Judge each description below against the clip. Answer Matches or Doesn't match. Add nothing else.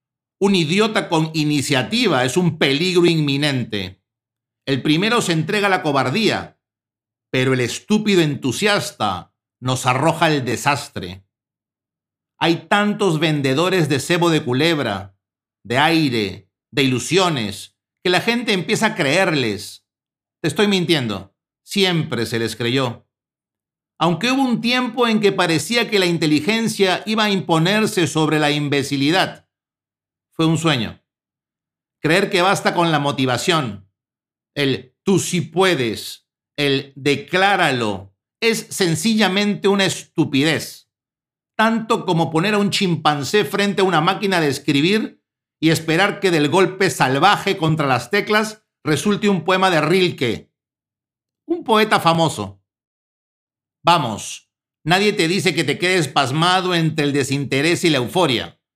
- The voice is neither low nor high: Matches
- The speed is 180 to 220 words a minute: Doesn't match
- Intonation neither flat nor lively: Doesn't match